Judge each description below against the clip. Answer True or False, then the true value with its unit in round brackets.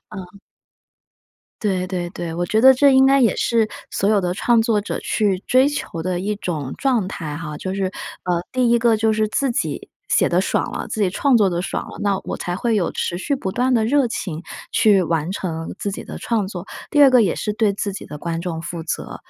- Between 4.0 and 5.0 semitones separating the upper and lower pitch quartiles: True (4.7 semitones)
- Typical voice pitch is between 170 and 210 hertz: True (200 Hz)